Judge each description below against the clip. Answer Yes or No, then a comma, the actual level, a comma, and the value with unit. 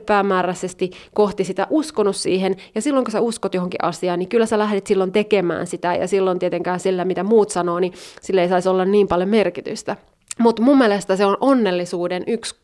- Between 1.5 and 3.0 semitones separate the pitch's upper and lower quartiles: Yes, average, 2.7 semitones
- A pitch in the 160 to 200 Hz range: Yes, high, 190 Hz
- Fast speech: Yes, fast, 195 wpm